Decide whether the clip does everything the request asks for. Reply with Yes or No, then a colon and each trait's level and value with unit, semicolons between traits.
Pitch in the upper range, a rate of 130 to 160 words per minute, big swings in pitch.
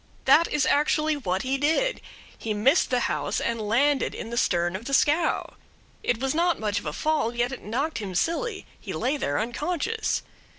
No: very high, 265 Hz; average, 195 wpm; wide, 5.9 semitones